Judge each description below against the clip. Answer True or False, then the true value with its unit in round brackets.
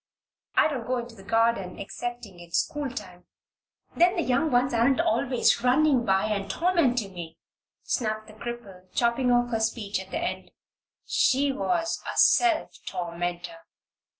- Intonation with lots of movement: True (5.7 semitones)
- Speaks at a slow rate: False (150 wpm)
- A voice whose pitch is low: False (240 Hz)